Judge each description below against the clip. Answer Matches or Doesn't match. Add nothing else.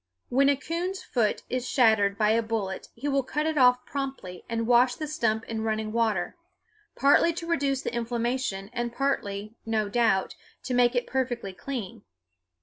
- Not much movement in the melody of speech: Doesn't match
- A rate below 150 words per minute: Doesn't match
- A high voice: Matches